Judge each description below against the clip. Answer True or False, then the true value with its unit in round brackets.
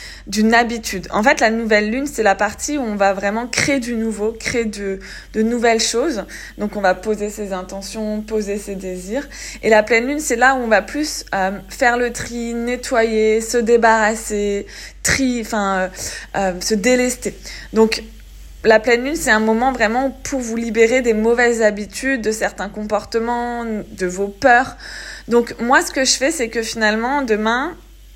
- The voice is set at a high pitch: True (225 Hz)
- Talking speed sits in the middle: True (180 wpm)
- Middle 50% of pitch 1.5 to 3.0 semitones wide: True (2.6 semitones)